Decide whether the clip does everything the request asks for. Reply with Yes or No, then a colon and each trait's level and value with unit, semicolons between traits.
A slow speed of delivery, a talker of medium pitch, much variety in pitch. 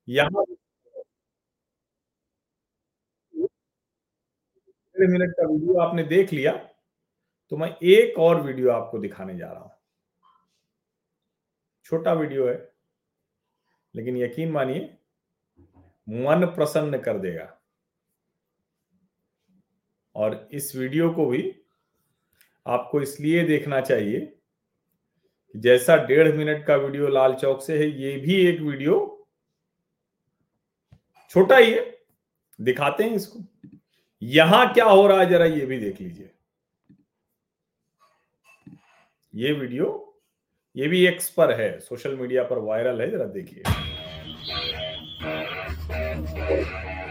Yes: slow, 100 wpm; medium, 160 Hz; wide, 7.7 semitones